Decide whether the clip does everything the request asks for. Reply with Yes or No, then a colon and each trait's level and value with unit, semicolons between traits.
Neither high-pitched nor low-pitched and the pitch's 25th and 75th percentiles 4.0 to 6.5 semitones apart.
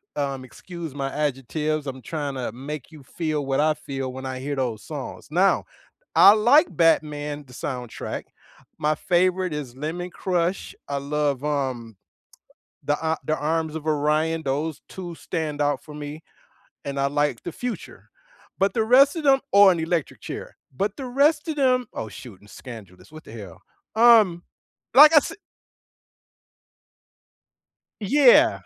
Yes: medium, 150 Hz; average, 4.9 semitones